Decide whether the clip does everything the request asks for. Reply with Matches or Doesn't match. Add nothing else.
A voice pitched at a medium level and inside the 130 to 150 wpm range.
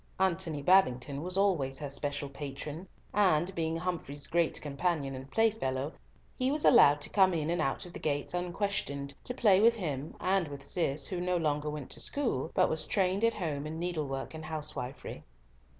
Doesn't match